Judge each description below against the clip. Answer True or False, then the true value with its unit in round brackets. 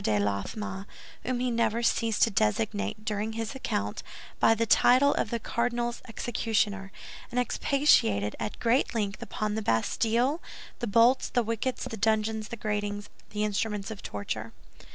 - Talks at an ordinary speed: True (155 wpm)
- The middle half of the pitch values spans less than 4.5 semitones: True (2.7 semitones)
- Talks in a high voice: True (220 Hz)